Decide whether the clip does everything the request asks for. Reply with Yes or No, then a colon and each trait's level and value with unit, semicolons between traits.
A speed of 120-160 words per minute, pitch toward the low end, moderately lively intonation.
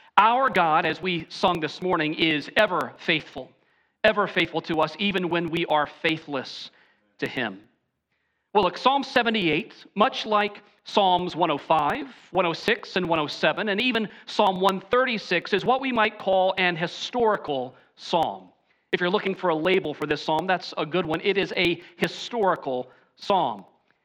No: average, 155 wpm; medium, 180 Hz; average, 4.3 semitones